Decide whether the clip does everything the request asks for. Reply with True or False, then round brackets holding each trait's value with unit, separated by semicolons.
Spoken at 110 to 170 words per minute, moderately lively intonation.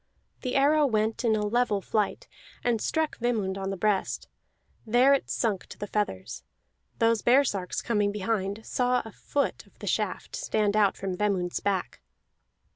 True (160 wpm; 3.5 semitones)